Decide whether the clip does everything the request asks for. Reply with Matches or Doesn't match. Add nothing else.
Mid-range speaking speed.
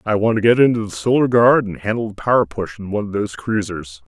Doesn't match